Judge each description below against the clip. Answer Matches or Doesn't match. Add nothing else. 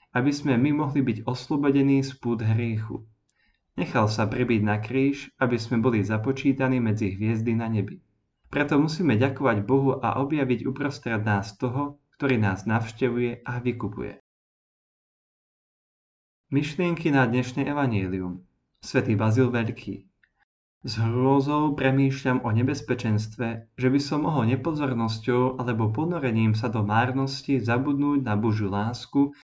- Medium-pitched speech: Doesn't match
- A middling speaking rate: Matches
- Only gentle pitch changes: Doesn't match